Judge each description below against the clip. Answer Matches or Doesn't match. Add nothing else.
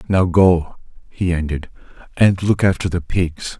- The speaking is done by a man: Matches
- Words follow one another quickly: Doesn't match